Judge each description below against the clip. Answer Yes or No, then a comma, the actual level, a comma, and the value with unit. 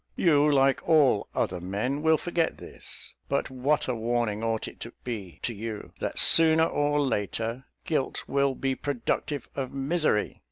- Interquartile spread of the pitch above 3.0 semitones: Yes, average, 4.4 semitones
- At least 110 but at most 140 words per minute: No, average, 160 wpm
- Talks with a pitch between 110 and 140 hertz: Yes, low, 135 Hz